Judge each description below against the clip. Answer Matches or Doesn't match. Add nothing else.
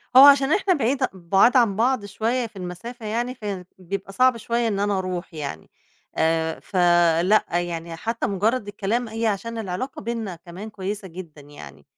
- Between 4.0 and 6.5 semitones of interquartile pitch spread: Matches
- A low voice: Doesn't match